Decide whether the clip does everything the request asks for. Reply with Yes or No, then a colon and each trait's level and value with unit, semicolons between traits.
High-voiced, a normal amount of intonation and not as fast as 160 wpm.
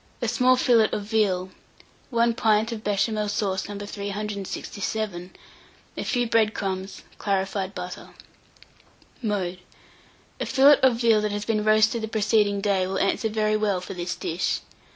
No: high, 210 Hz; narrow, 2.1 semitones; average, 150 wpm